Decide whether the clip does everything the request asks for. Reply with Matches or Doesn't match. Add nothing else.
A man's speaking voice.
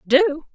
Doesn't match